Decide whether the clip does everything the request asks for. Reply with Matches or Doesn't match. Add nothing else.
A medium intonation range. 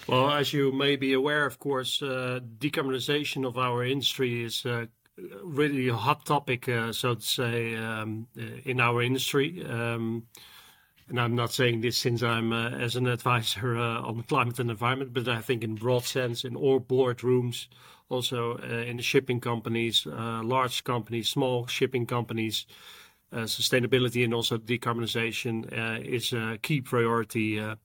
Doesn't match